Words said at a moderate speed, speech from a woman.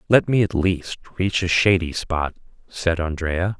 No: average, 165 wpm; male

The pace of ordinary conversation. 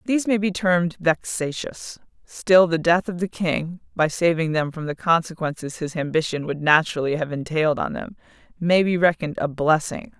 Yes: average, 175 wpm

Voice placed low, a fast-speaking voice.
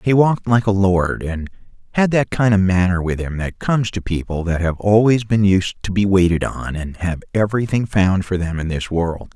Yes: very low, 95 Hz; fast, 225 wpm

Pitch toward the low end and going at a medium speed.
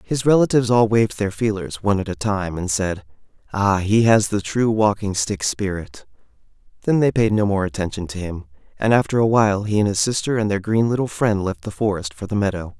No: low, 105 Hz; fast, 220 wpm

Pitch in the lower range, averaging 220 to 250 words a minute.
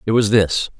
Yes: low, 105 Hz; fast, 225 wpm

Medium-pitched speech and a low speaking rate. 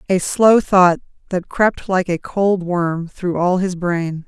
No: medium, 180 Hz; average, 185 wpm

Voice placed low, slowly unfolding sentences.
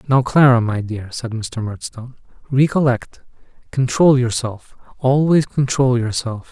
Yes: low, 125 Hz; slow, 120 wpm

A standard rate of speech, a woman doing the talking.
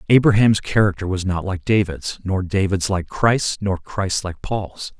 No: average, 170 wpm; male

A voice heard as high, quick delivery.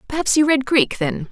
Yes: very high, 260 Hz; fast, 230 wpm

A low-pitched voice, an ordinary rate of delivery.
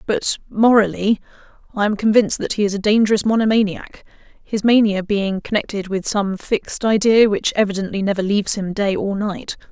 No: high, 205 Hz; average, 165 wpm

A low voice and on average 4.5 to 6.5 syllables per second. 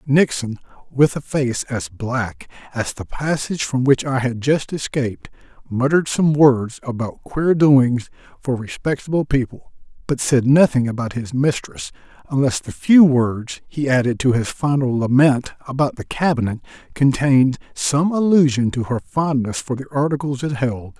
Yes: low, 130 Hz; 4.6 syllables/s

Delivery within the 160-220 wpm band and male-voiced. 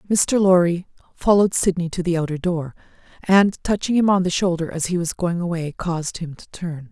No: average, 200 wpm; female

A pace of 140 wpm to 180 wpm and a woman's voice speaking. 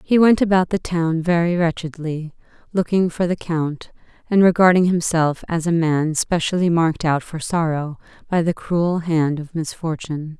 Yes: average, 160 wpm; female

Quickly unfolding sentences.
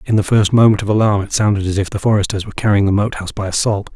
Yes: fast, 290 wpm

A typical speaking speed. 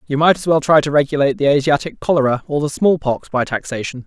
No: fast, 235 wpm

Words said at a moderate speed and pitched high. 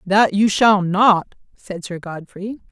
Yes: average, 155 wpm; high, 195 Hz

